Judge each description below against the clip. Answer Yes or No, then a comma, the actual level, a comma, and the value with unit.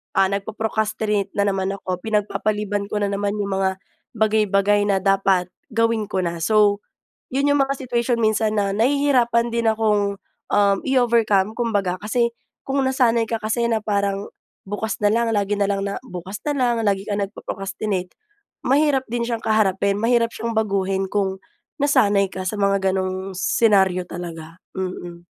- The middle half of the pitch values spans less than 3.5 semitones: Yes, average, 2.7 semitones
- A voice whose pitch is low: No, high, 205 Hz